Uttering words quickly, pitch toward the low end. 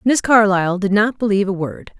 No: fast, 210 wpm; high, 205 Hz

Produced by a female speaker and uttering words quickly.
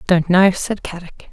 No: female; average, 180 wpm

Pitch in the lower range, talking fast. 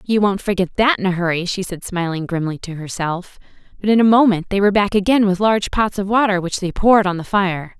No: high, 190 Hz; fast, 245 wpm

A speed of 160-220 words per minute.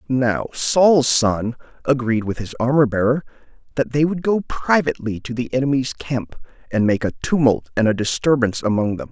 Yes: average, 170 wpm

